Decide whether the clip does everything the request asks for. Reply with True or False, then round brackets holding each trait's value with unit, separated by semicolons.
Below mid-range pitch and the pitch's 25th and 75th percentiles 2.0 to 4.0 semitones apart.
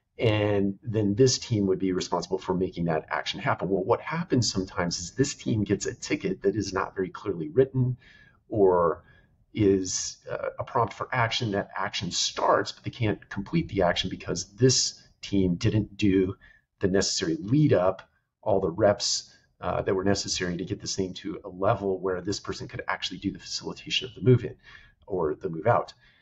True (100 Hz; 3.7 semitones)